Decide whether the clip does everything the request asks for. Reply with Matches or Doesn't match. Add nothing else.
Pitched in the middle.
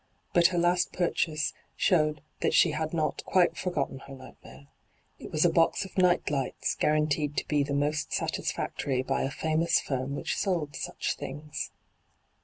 Matches